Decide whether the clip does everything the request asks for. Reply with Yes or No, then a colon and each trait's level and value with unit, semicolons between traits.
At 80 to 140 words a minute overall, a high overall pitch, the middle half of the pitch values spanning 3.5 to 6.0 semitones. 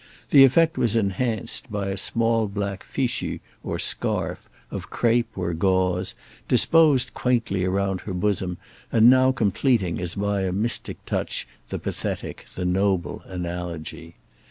No: slow, 135 wpm; low, 100 Hz; average, 4.3 semitones